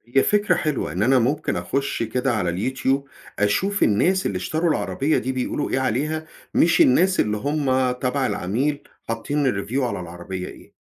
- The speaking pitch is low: Yes, low, 130 Hz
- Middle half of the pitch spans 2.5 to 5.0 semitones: No, wide, 5.6 semitones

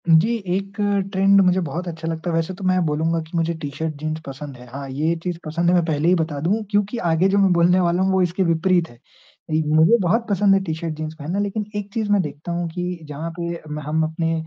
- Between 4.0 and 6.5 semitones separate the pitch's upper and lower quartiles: No, average, 3.1 semitones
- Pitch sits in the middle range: Yes, medium, 170 Hz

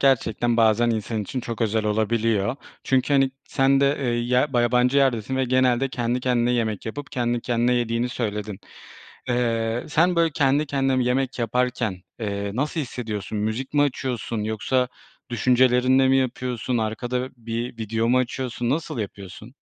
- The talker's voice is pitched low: Yes, low, 120 Hz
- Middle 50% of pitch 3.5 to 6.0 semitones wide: No, narrow, 2.5 semitones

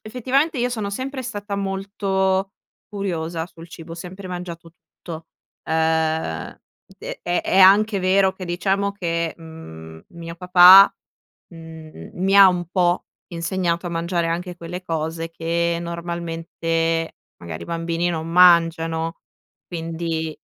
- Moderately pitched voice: Yes, medium, 170 Hz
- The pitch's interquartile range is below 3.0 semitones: Yes, narrow, 2.6 semitones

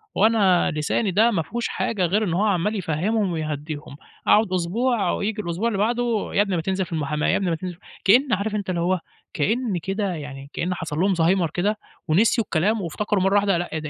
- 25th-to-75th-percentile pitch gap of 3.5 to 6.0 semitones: Yes, average, 4.1 semitones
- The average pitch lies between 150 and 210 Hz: Yes, high, 190 Hz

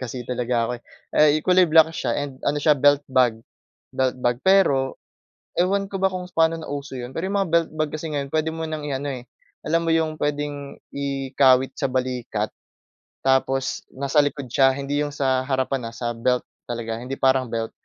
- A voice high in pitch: No, medium, 140 Hz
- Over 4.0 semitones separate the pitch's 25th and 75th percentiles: No, average, 3.4 semitones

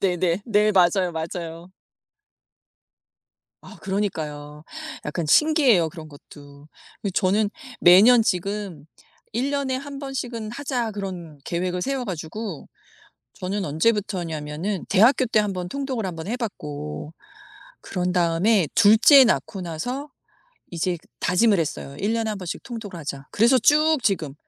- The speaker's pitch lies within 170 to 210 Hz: Yes, high, 190 Hz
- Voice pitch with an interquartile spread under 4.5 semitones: No, wide, 5.6 semitones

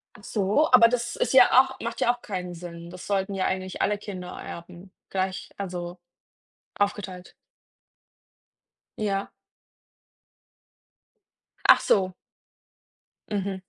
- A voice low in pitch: No, high, 195 Hz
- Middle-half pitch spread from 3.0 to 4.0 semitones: No, narrow, 2.4 semitones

